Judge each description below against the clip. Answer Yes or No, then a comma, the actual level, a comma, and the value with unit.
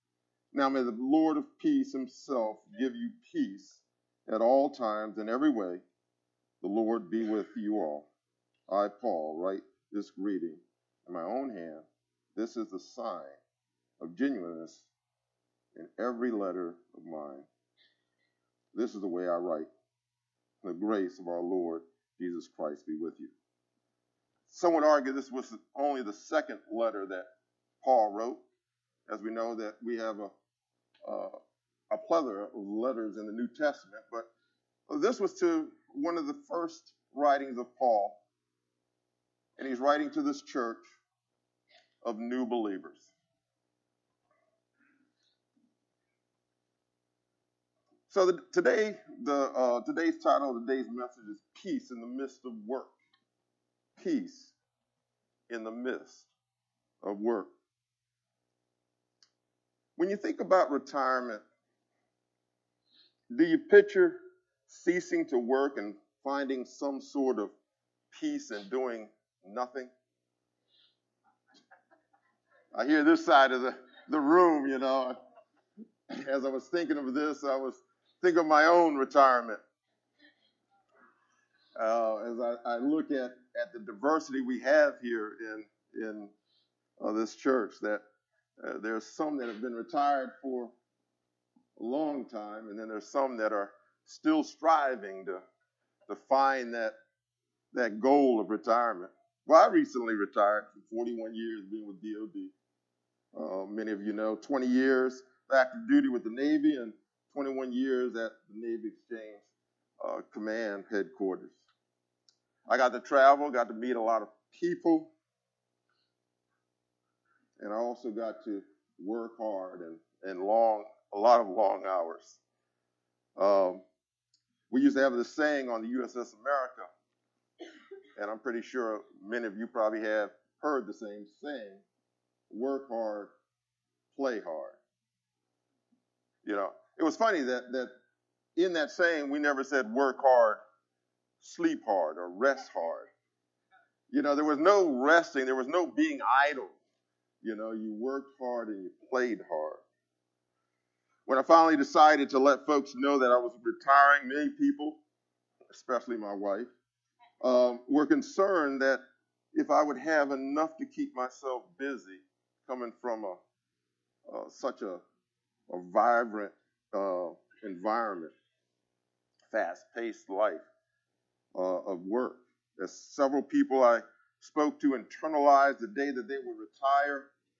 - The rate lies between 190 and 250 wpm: No, slow, 135 wpm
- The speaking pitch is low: Yes, low, 115 Hz